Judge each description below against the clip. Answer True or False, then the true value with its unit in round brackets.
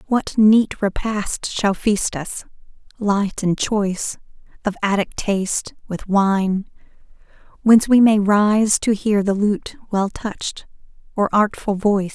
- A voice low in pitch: False (205 Hz)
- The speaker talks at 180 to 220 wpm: False (135 wpm)